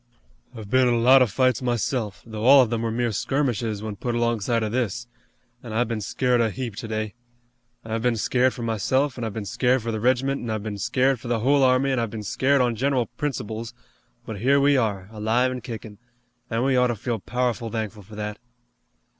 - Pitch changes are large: No, narrow, 2.6 semitones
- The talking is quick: Yes, fast, 220 wpm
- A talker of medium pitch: No, low, 120 Hz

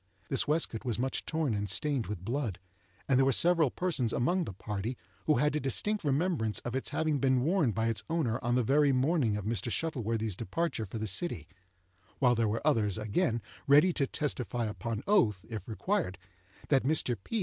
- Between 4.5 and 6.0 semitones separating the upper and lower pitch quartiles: Yes, wide, 5.4 semitones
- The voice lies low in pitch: Yes, low, 125 Hz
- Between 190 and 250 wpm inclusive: Yes, average, 195 wpm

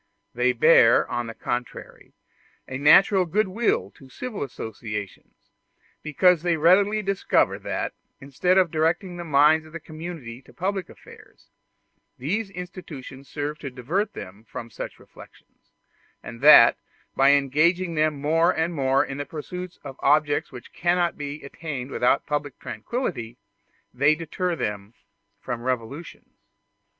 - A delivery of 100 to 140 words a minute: Yes, slow, 135 wpm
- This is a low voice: No, medium, 150 Hz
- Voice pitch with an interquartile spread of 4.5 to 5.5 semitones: Yes, average, 5.1 semitones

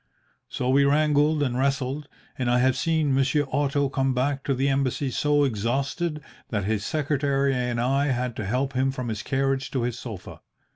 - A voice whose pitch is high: No, low, 135 Hz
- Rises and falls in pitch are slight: Yes, narrow, 2.2 semitones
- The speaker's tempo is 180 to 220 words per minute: Yes, average, 185 wpm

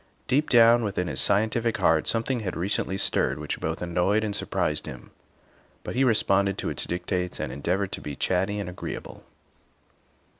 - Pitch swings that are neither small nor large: Yes, average, 3.8 semitones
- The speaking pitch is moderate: No, very low, 95 Hz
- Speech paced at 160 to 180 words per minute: Yes, average, 165 wpm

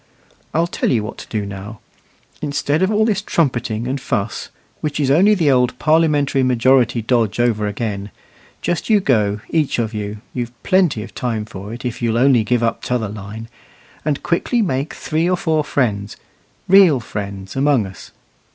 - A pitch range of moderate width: No, wide, 5.9 semitones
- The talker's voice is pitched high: No, low, 125 Hz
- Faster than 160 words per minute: Yes, average, 175 wpm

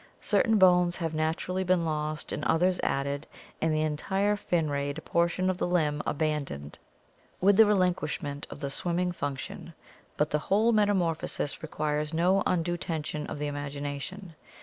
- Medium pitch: Yes, medium, 160 Hz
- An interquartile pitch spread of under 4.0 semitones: Yes, average, 3.5 semitones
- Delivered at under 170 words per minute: Yes, average, 155 wpm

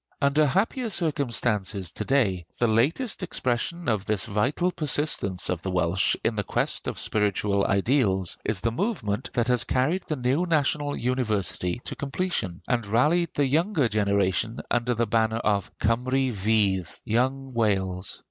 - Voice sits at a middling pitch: No, low, 120 Hz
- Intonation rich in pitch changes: Yes, wide, 5.8 semitones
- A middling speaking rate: Yes, average, 150 wpm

